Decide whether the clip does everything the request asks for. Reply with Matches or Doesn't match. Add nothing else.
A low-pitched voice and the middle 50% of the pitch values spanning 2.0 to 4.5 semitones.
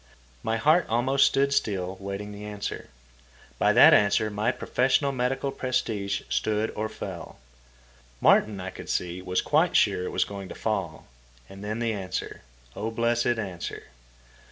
Matches